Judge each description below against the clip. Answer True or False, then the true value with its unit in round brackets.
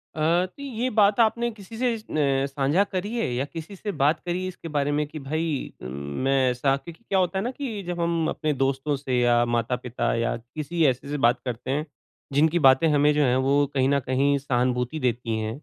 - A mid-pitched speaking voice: True (145 Hz)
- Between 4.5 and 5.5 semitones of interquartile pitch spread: True (5.0 semitones)